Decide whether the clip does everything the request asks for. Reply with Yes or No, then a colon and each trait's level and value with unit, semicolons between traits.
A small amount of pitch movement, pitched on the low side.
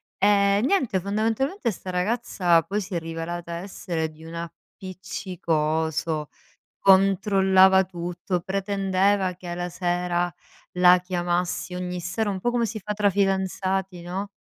No: narrow, 2.2 semitones; medium, 185 Hz